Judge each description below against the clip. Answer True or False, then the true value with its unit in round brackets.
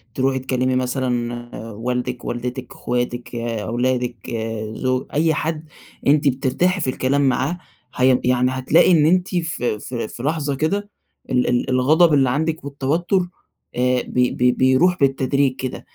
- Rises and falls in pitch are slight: False (3.1 semitones)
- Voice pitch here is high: False (130 Hz)